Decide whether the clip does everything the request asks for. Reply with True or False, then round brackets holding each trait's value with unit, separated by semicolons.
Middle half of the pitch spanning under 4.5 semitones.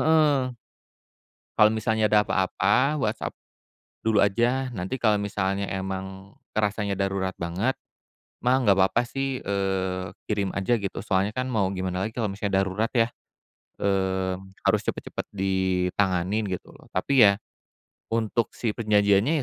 True (2.9 semitones)